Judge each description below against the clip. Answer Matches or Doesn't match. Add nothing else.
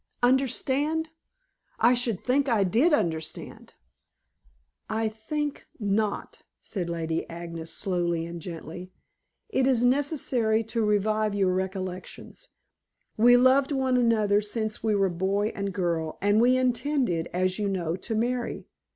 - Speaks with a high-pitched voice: Matches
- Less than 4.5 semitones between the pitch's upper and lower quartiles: Doesn't match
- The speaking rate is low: Matches